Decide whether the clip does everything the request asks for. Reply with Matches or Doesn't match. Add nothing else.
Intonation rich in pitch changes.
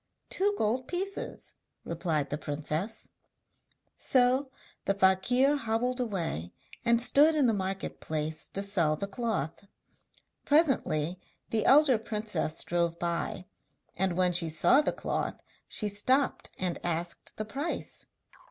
Matches